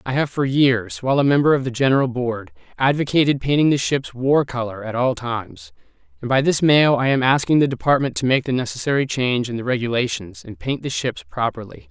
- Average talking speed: No, fast, 210 wpm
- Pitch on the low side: Yes, low, 130 Hz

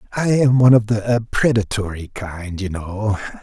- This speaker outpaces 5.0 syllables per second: No, 4.6 syllables/s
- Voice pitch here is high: No, low, 110 Hz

